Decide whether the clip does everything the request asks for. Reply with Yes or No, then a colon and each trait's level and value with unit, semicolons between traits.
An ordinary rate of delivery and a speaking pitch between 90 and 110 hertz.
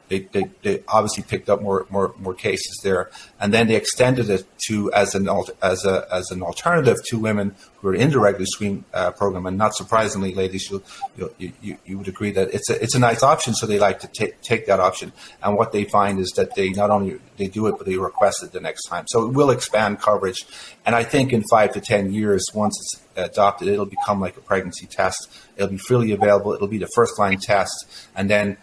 No: fast, 235 wpm; low, 100 Hz